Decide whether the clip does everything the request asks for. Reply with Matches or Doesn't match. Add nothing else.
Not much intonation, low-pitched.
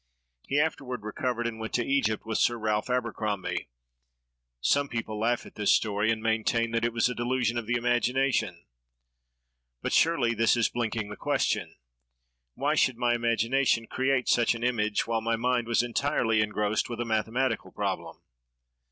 Matches